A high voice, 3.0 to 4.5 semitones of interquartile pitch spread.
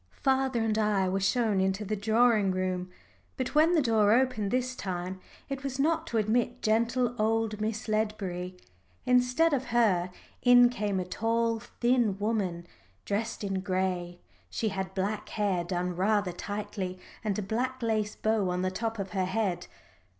Yes: high, 215 Hz; average, 3.9 semitones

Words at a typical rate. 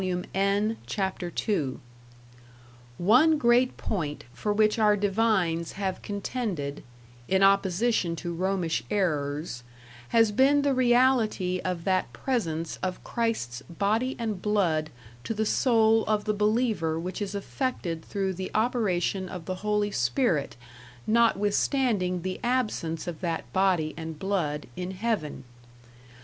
No: slow, 125 wpm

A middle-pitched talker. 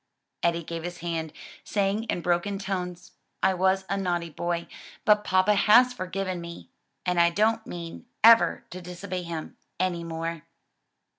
Yes: medium, 180 Hz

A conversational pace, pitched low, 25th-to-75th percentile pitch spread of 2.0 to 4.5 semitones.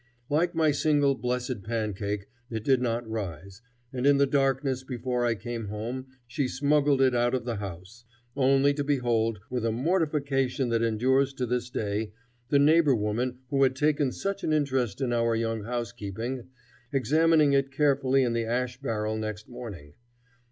Yes: average, 165 wpm; low, 125 Hz; average, 3.4 semitones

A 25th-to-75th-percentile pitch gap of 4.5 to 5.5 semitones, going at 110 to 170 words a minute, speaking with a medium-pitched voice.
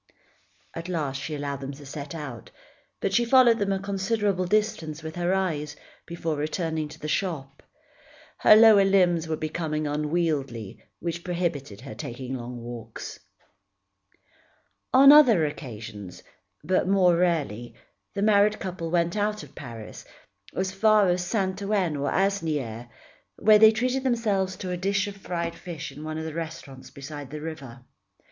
Yes: average, 5.1 semitones; average, 155 wpm; medium, 170 Hz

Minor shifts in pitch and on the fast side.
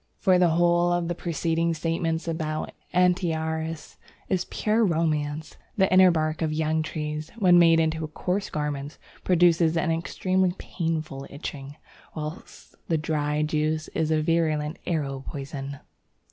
No: narrow, 2.1 semitones; slow, 135 wpm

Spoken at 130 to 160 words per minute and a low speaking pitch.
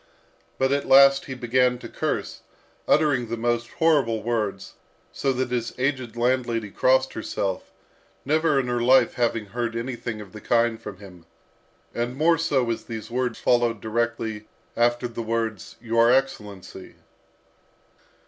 Yes: average, 145 wpm; low, 120 Hz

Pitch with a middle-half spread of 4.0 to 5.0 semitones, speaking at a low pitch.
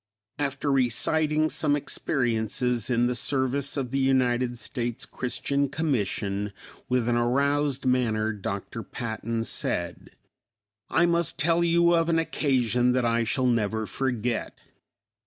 No: average, 3.4 semitones; low, 125 Hz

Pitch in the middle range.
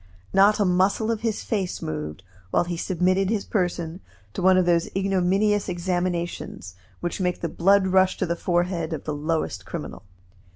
Yes: medium, 180 Hz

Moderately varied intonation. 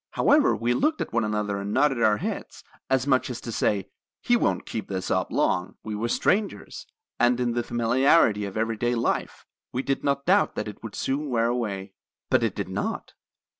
Yes: average, 4.0 semitones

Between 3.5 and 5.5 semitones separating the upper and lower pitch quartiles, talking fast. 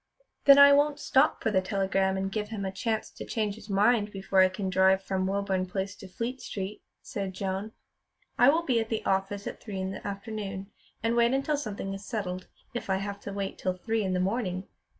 No: average, 2.7 semitones; fast, 220 wpm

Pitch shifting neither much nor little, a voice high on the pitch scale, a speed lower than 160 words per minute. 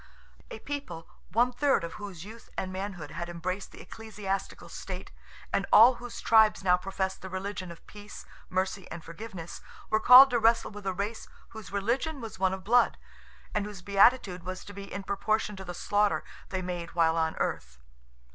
No: average, 3.2 semitones; high, 200 Hz; average, 185 wpm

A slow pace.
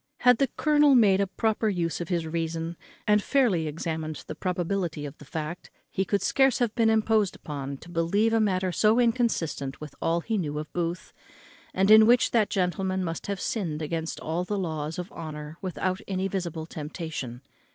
No: average, 185 wpm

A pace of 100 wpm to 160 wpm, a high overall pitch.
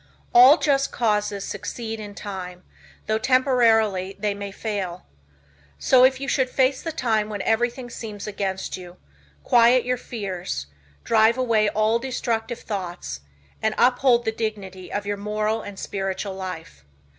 Yes: average, 145 wpm; high, 215 Hz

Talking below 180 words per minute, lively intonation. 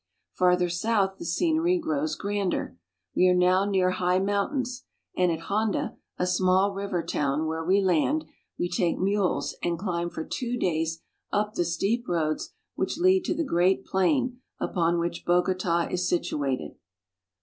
No: average, 155 wpm; average, 3.5 semitones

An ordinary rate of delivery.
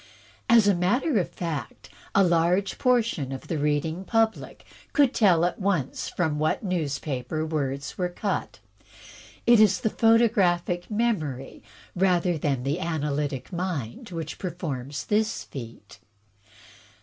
No: slow, 125 wpm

